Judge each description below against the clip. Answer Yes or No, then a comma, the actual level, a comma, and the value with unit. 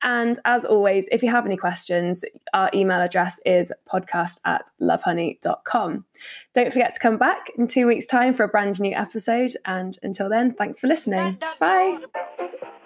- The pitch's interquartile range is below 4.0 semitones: No, average, 4.8 semitones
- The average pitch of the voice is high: Yes, high, 225 Hz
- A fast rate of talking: No, average, 170 wpm